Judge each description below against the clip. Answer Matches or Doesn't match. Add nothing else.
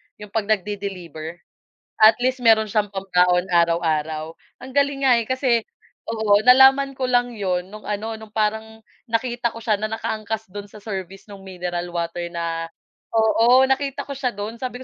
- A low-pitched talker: Doesn't match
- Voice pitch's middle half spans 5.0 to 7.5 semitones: Doesn't match